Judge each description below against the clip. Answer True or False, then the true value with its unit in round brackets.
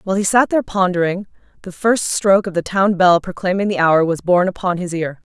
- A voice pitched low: False (185 Hz)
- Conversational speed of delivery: False (225 wpm)